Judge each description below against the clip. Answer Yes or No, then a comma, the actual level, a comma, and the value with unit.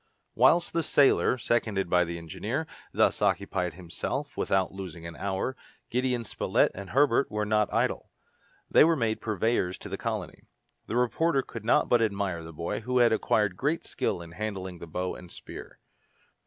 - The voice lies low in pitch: Yes, low, 105 Hz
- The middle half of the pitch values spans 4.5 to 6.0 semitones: Yes, wide, 5.4 semitones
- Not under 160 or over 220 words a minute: Yes, average, 170 wpm